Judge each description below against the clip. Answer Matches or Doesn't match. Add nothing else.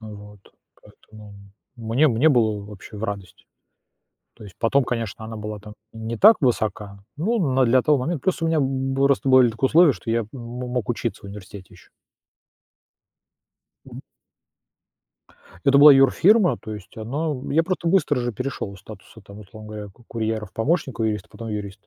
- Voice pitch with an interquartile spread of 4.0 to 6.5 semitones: Matches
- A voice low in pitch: Matches